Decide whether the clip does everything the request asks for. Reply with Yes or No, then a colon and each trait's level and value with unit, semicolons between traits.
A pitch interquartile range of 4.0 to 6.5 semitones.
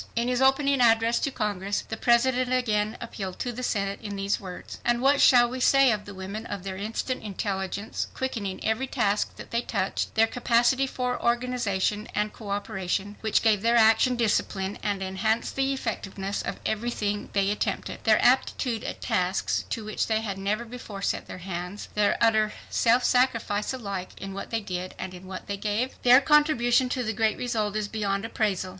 No: average, 3.3 semitones